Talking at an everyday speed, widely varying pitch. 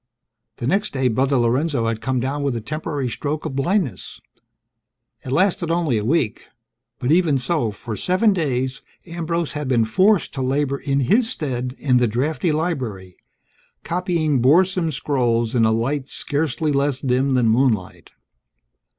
No: average, 155 wpm; average, 4.6 semitones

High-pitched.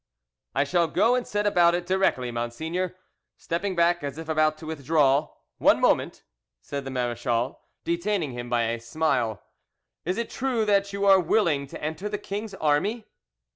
No: medium, 160 Hz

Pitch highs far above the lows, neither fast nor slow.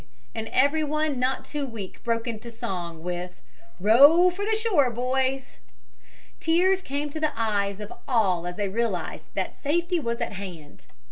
Yes: wide, 7.0 semitones; average, 155 wpm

